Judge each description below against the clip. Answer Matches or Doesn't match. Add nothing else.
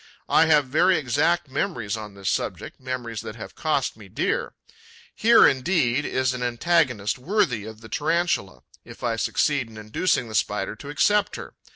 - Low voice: Matches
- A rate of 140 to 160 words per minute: Doesn't match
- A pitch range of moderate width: Doesn't match